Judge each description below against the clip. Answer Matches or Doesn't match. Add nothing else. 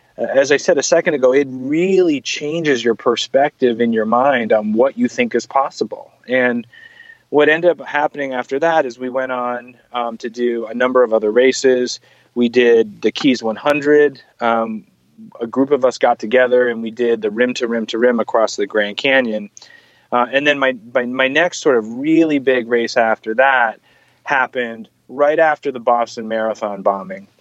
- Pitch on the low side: Matches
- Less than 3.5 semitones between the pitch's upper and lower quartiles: Doesn't match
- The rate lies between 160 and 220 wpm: Matches